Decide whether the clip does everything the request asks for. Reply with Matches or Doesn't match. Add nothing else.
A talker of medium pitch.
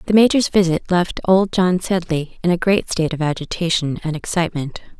Matches